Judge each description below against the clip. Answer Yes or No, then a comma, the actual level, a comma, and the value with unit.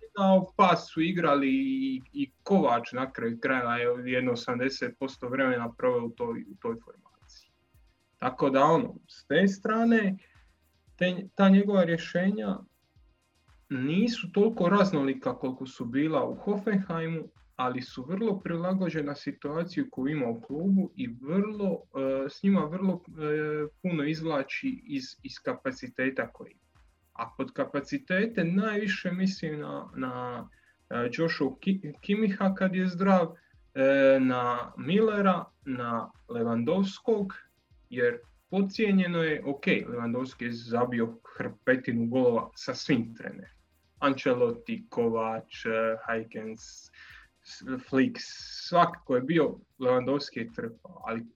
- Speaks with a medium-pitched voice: Yes, medium, 160 Hz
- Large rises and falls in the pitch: Yes, wide, 7.3 semitones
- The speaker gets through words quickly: No, average, 120 wpm